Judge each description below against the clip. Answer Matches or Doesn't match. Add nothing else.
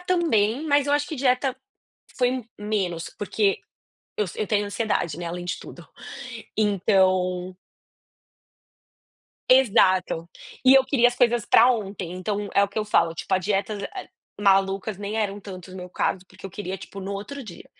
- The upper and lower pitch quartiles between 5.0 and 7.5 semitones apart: Doesn't match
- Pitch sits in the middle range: Doesn't match